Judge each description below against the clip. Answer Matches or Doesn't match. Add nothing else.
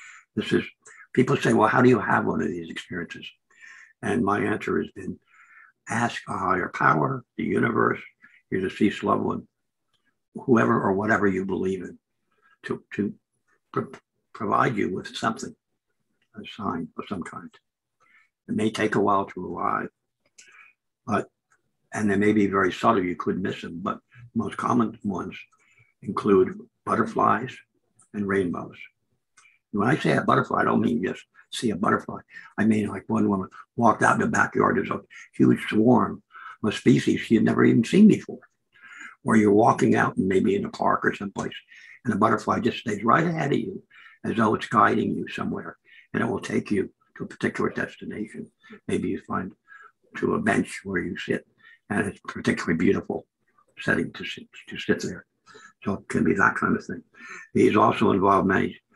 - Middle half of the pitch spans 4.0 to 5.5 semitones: Matches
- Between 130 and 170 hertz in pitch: Doesn't match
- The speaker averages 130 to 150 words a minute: Doesn't match